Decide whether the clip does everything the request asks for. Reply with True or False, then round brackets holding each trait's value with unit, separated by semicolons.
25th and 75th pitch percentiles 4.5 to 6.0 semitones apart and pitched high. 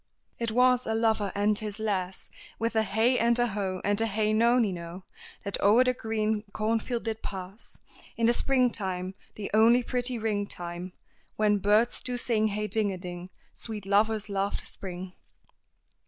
False (2.6 semitones; 215 Hz)